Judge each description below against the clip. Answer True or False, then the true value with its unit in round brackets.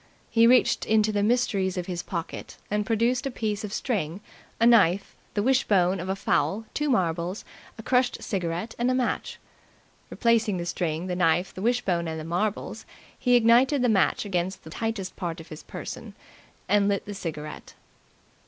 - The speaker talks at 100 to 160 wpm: False (175 wpm)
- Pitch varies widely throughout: False (4.7 semitones)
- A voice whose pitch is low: False (200 Hz)